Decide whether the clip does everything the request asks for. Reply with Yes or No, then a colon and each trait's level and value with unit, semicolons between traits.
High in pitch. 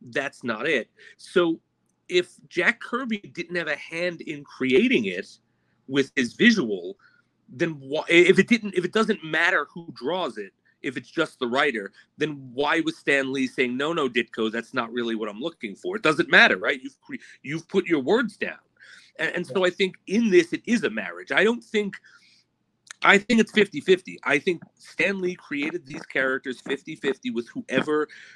No: medium, 180 Hz